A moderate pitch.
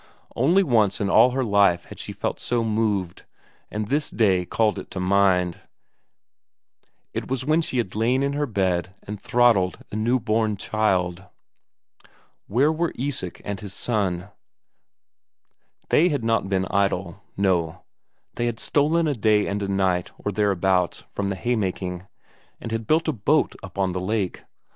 No: low, 105 Hz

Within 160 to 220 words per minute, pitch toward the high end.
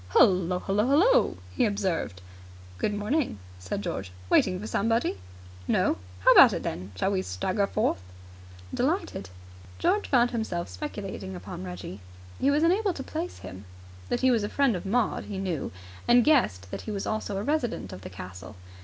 Yes: average, 170 wpm; high, 205 Hz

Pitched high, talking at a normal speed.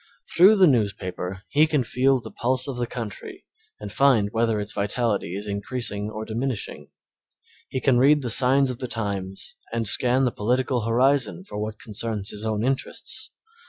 No: low, 115 Hz; average, 170 wpm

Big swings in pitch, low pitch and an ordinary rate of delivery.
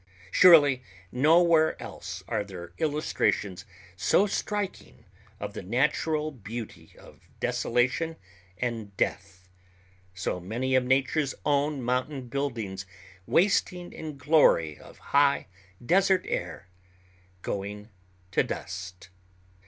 No: wide, 7.9 semitones; low, 125 Hz; slow, 100 wpm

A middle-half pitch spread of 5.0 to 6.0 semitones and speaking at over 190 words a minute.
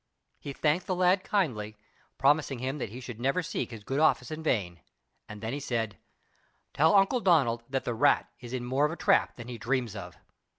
Yes: average, 5.3 semitones; fast, 205 wpm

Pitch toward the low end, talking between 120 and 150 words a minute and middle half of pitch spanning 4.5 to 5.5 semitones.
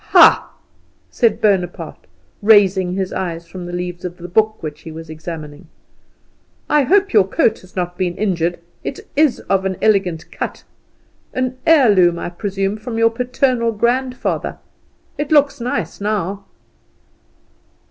No: high, 195 Hz; average, 140 wpm; average, 4.9 semitones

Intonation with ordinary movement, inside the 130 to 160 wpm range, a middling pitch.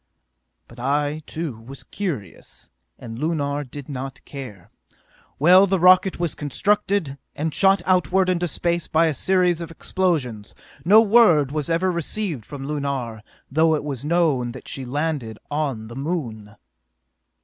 Yes: average, 4.9 semitones; average, 145 wpm; medium, 150 Hz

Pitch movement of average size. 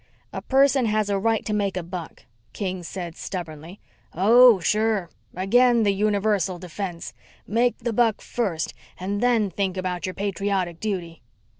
Yes: average, 3.3 semitones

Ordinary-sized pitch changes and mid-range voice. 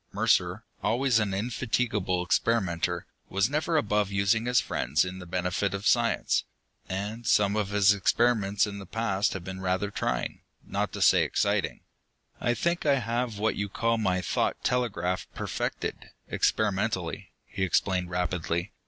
No: average, 3.7 semitones; low, 100 Hz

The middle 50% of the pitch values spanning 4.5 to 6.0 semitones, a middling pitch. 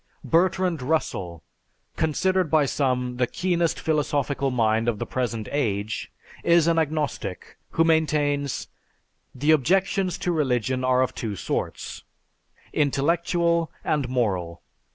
Yes: average, 4.8 semitones; medium, 145 Hz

